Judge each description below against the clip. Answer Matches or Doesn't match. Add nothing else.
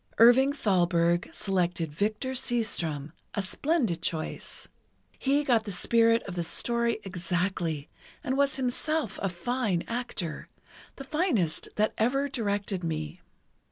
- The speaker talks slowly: Matches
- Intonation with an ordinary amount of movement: Doesn't match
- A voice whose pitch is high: Matches